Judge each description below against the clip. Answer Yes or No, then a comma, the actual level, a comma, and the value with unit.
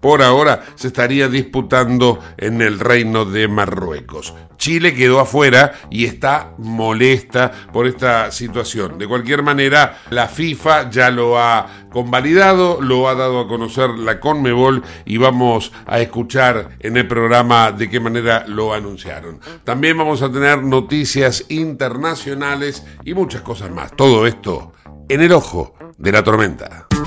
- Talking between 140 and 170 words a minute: Yes, average, 145 wpm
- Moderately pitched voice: No, low, 120 Hz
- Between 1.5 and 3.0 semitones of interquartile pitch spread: No, average, 3.4 semitones